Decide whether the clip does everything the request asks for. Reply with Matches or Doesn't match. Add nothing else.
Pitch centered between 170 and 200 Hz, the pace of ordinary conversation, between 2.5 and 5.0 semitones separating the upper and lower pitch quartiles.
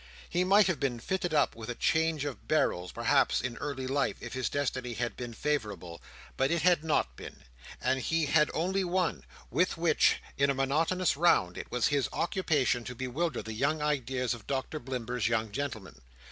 Doesn't match